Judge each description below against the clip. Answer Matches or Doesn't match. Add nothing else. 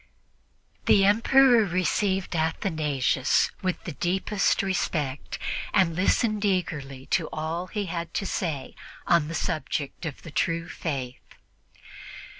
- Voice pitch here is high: Doesn't match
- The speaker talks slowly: Matches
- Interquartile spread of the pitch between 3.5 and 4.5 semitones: Matches